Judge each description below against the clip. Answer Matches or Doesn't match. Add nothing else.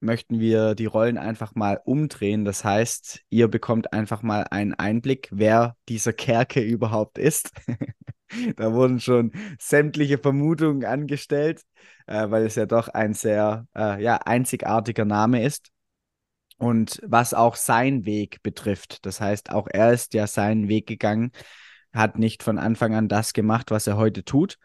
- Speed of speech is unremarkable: Matches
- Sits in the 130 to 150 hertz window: Doesn't match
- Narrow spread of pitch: Matches